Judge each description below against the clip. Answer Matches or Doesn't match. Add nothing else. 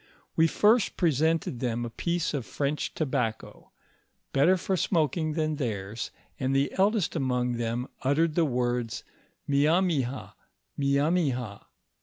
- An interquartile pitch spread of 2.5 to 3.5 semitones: Doesn't match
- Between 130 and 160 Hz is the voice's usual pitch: Matches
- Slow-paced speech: Matches